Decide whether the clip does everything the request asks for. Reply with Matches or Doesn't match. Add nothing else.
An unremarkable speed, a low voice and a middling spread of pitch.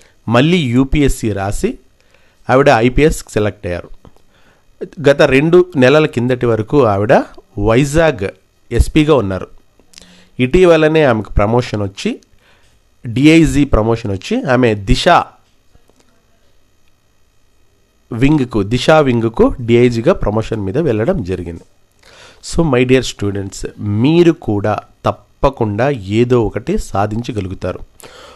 Doesn't match